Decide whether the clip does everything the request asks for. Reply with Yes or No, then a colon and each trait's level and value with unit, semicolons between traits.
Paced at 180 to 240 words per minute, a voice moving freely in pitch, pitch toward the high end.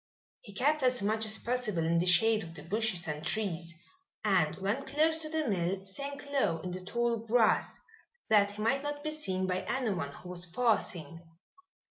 Yes: average, 185 wpm; wide, 5.7 semitones; high, 210 Hz